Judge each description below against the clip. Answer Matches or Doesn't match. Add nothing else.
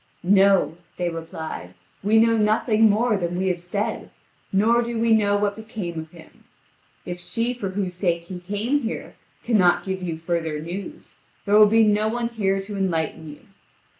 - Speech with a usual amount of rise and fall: Matches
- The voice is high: Matches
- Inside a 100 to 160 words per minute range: Doesn't match